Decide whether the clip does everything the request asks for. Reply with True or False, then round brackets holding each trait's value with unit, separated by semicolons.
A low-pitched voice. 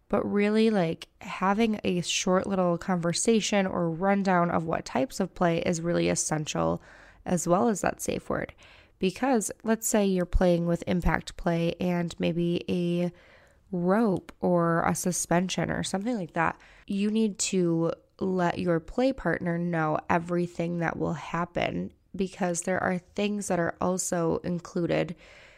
False (175 Hz)